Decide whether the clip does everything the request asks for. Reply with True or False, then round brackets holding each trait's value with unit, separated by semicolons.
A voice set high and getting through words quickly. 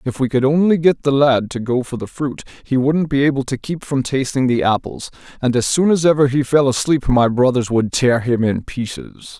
False (135 Hz; 235 wpm)